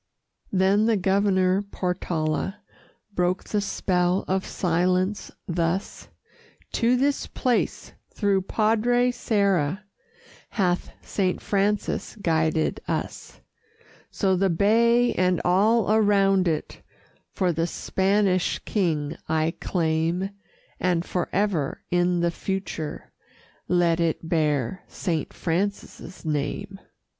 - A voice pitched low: No, medium, 185 Hz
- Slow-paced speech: Yes, slow, 100 wpm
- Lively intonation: No, average, 3.1 semitones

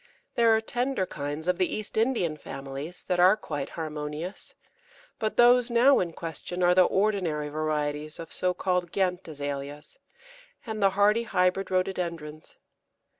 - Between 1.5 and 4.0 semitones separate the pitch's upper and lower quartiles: No, average, 4.9 semitones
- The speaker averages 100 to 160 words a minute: Yes, average, 145 wpm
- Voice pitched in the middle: Yes, medium, 180 Hz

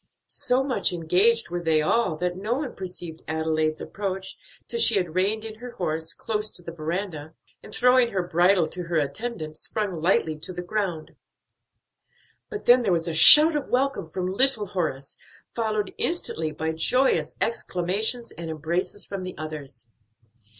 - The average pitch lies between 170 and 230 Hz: Yes, medium, 185 Hz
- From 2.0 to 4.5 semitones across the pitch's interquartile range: No, wide, 5.5 semitones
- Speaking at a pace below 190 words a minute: Yes, average, 165 wpm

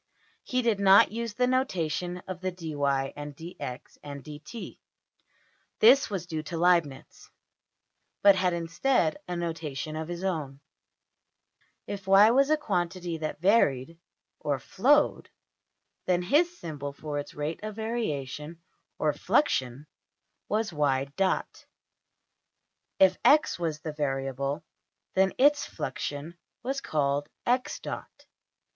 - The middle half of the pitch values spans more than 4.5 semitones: Yes, wide, 5.6 semitones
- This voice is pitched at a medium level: Yes, medium, 170 Hz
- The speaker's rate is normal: No, slow, 115 wpm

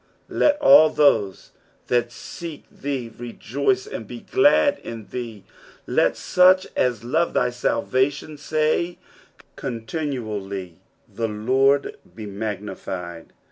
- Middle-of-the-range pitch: No, low, 125 Hz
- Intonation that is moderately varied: No, wide, 6.1 semitones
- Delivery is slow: Yes, slow, 110 wpm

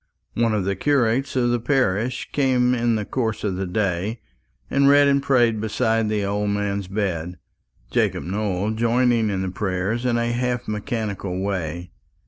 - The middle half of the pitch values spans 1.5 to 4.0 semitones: Yes, average, 3.7 semitones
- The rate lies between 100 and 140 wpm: No, average, 165 wpm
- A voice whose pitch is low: Yes, low, 110 Hz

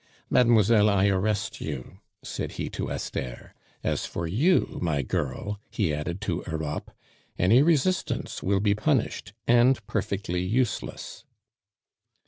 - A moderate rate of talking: No, slow, 120 wpm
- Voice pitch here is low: Yes, low, 100 Hz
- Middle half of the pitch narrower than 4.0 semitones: No, wide, 5.4 semitones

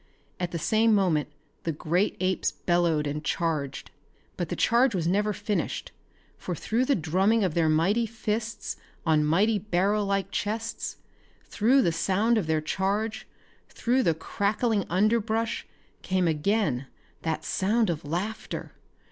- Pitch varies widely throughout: No, average, 4.9 semitones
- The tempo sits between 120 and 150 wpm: Yes, average, 140 wpm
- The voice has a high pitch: Yes, high, 195 Hz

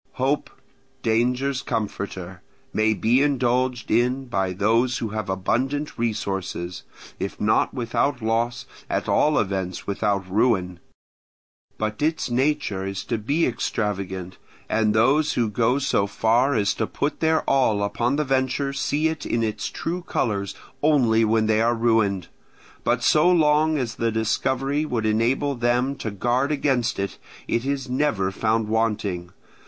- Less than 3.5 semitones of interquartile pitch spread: No, average, 4.2 semitones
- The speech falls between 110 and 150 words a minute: Yes, average, 145 wpm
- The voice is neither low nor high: No, low, 115 Hz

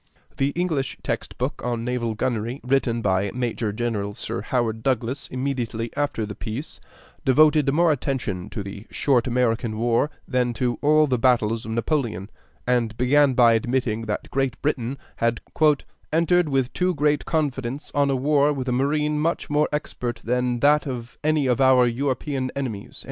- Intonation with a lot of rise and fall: No, average, 3.6 semitones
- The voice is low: Yes, low, 125 Hz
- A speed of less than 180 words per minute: Yes, average, 160 wpm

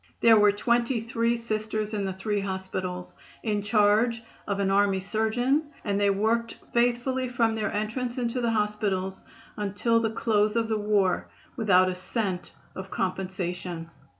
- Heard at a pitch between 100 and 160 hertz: No, high, 210 Hz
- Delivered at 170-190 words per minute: No, average, 150 wpm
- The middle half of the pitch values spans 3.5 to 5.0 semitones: No, average, 3.0 semitones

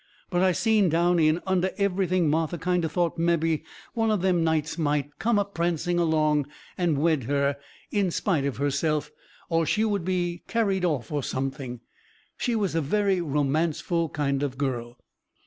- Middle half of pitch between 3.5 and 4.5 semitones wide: Yes, average, 3.9 semitones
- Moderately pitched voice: Yes, medium, 165 Hz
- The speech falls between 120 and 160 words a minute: No, average, 170 wpm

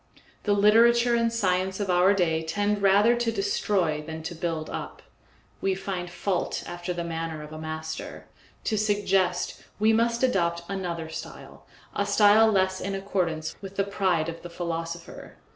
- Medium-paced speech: Yes, average, 160 wpm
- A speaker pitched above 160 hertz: Yes, high, 190 Hz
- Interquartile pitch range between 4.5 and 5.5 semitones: No, average, 3.4 semitones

